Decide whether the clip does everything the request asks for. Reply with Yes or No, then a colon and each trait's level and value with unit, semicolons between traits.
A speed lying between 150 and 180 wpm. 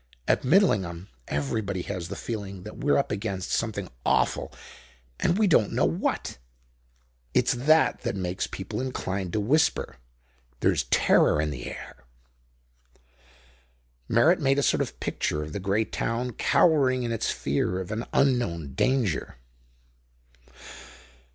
No: slow, 135 wpm